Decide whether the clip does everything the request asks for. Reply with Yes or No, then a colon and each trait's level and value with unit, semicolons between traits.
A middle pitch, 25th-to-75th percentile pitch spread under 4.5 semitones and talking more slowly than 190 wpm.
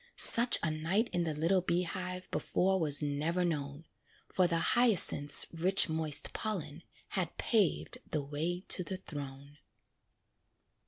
Yes: medium, 170 Hz; average, 3.7 semitones; average, 140 wpm